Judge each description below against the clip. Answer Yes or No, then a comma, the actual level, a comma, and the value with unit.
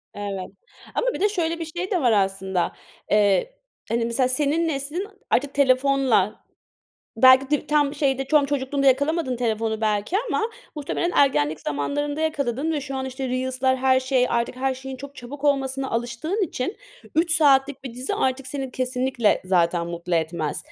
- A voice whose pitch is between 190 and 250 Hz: No, very high, 265 Hz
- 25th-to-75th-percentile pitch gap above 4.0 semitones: No, average, 3.7 semitones